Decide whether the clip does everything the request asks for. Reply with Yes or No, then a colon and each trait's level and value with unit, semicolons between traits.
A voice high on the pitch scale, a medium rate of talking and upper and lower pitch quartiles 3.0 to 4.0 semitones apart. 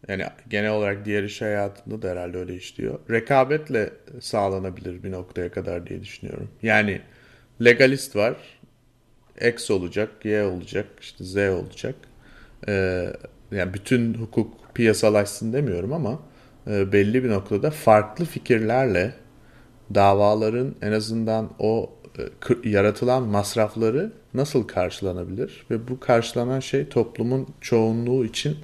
No: low, 110 Hz; average, 110 wpm; average, 3.5 semitones